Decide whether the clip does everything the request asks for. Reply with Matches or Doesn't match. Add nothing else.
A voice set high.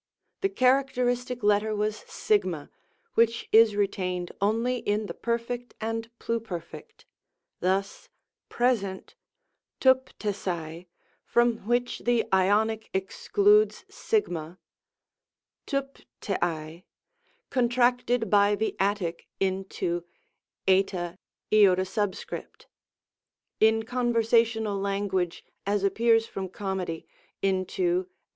Matches